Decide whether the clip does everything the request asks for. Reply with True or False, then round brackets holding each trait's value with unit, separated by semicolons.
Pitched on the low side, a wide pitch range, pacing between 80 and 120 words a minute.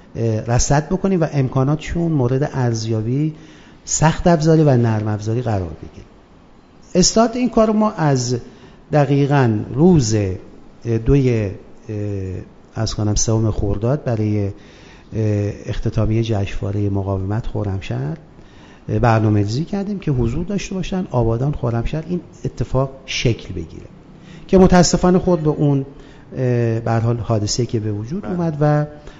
True (120 Hz; 6.3 semitones; 110 wpm)